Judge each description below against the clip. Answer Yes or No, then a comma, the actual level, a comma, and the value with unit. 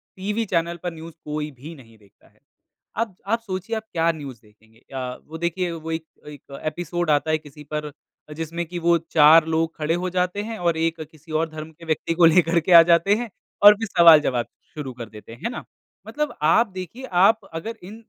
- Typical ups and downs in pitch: Yes, average, 3.1 semitones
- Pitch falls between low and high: Yes, medium, 165 Hz